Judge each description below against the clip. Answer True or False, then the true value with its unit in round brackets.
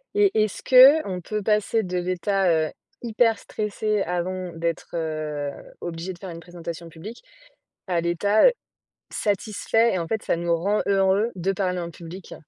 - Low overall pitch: False (185 Hz)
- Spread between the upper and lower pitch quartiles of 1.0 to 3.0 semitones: False (3.8 semitones)